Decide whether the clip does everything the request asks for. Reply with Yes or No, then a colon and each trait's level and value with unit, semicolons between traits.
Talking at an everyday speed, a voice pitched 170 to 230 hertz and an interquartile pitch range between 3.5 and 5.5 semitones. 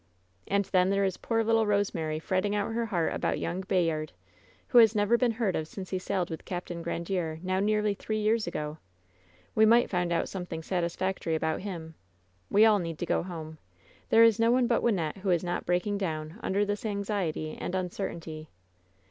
Yes: average, 195 wpm; high, 190 Hz; average, 3.8 semitones